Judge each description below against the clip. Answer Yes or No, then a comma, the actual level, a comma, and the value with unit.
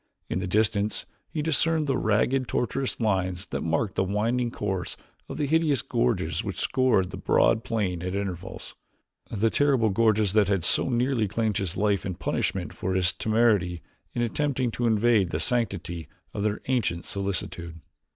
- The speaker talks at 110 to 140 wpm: No, average, 165 wpm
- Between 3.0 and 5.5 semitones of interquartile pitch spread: Yes, average, 4.2 semitones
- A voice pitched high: No, low, 105 Hz